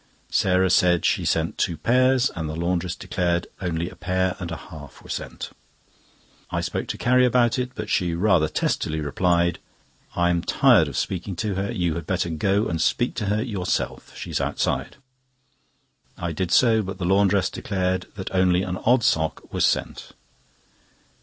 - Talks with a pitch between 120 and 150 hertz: No, very low, 90 Hz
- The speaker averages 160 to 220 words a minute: Yes, average, 175 wpm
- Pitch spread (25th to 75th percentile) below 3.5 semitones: Yes, average, 3.1 semitones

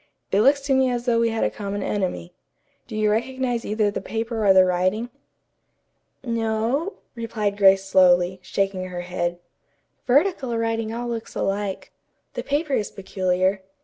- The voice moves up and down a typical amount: Yes, average, 3.7 semitones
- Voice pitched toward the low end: No, high, 215 Hz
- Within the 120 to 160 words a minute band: Yes, average, 155 wpm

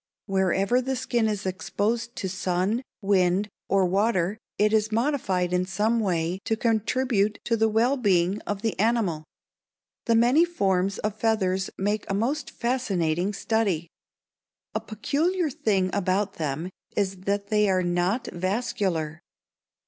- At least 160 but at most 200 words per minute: No, average, 140 wpm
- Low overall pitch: No, high, 205 Hz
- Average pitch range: Yes, average, 3.5 semitones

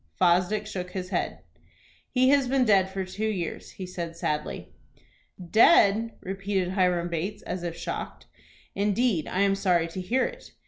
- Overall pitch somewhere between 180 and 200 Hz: Yes, high, 190 Hz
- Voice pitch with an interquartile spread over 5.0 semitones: No, average, 3.0 semitones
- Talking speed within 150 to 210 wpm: Yes, average, 155 wpm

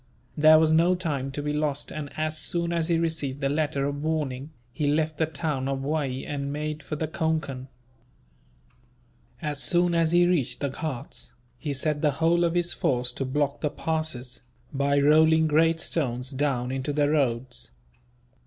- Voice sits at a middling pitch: Yes, medium, 150 Hz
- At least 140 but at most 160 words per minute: No, average, 175 wpm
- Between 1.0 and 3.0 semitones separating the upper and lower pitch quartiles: Yes, narrow, 2.5 semitones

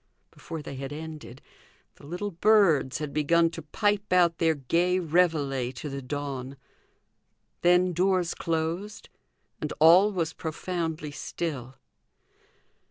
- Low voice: No, medium, 160 Hz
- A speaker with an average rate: No, slow, 120 wpm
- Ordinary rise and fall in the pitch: Yes, average, 3.6 semitones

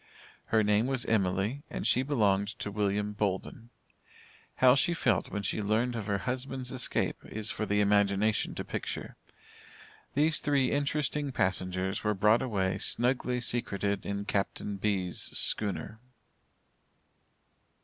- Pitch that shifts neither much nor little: Yes, average, 3.9 semitones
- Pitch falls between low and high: No, low, 105 Hz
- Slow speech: Yes, slow, 130 wpm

